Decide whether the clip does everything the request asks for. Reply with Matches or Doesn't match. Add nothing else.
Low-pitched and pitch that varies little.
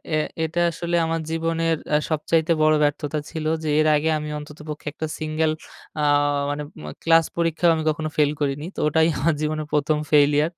Doesn't match